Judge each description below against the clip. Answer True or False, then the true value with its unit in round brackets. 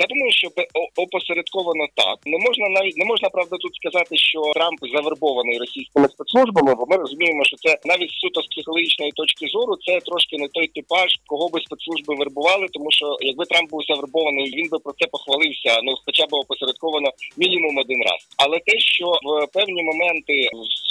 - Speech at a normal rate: False (180 wpm)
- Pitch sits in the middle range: True (160 Hz)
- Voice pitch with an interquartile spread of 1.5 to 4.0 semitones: True (3.3 semitones)